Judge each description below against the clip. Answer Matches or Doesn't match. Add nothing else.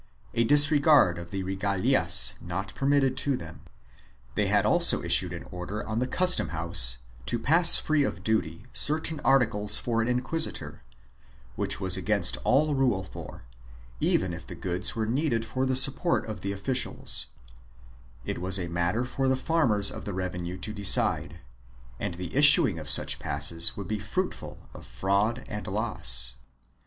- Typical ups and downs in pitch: Doesn't match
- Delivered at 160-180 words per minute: Matches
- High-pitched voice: Doesn't match